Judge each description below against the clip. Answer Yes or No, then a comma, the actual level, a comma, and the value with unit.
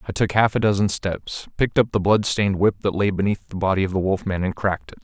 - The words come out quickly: Yes, fast, 285 wpm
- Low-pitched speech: Yes, low, 100 Hz